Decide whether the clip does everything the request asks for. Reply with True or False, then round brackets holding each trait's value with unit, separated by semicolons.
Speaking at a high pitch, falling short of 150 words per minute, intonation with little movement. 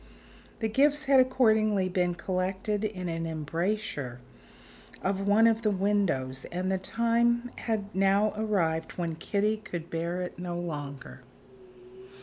False (195 Hz; 135 wpm; 4.0 semitones)